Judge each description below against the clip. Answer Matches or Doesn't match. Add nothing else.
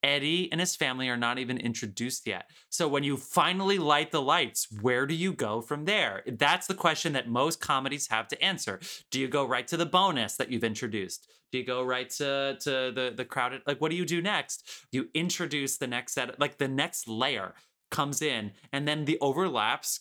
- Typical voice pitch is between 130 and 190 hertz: Matches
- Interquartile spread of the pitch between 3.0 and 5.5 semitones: Matches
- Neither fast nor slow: Doesn't match